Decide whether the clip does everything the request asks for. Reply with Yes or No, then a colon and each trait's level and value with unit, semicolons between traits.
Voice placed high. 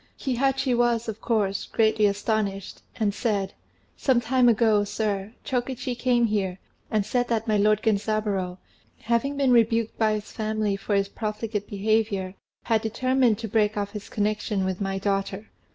Yes: high, 215 Hz